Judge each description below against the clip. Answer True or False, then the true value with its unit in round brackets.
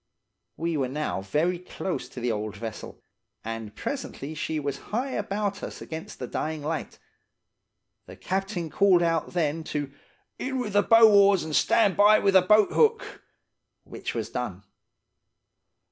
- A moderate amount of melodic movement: False (5.7 semitones)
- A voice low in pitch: False (170 Hz)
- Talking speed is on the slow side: False (155 wpm)